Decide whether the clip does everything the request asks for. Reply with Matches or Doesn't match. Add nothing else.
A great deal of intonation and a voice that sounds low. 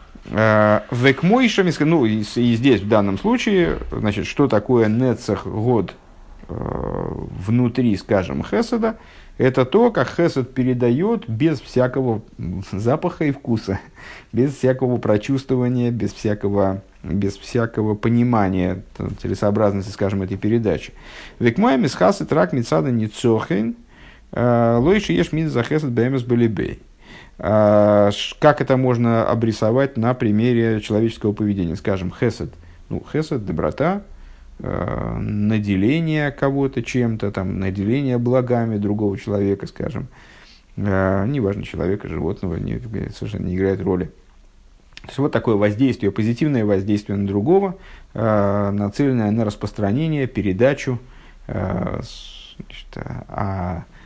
Doesn't match